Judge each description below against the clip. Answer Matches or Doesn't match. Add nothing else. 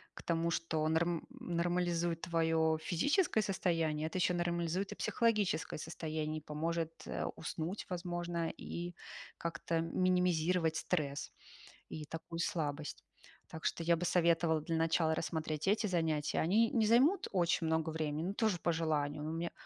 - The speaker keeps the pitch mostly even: Matches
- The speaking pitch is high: Doesn't match